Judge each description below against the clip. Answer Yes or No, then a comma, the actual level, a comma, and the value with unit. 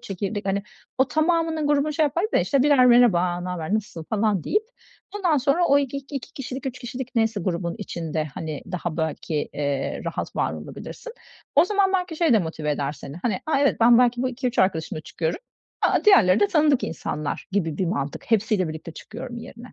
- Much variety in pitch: Yes, wide, 8.6 semitones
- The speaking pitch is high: Yes, high, 225 Hz